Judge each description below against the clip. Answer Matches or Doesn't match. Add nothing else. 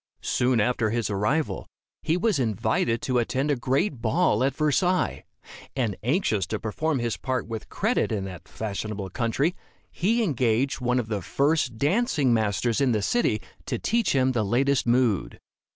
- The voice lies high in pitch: Doesn't match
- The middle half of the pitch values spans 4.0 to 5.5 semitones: Matches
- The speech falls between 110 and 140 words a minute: Doesn't match